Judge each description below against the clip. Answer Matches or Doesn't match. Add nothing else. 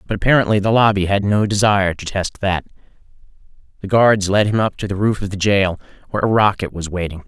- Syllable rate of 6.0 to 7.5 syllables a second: Matches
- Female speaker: Doesn't match